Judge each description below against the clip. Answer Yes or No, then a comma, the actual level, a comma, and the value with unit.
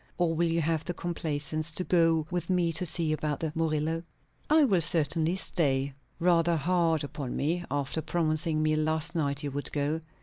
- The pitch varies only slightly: Yes, narrow, 2.0 semitones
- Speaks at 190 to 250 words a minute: No, average, 180 wpm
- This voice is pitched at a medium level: Yes, medium, 160 Hz